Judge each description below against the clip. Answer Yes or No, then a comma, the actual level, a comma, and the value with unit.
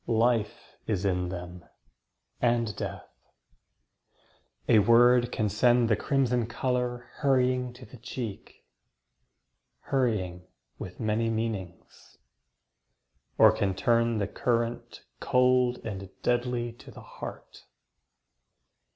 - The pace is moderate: No, slow, 100 wpm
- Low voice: Yes, low, 115 Hz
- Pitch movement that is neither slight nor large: Yes, average, 3.1 semitones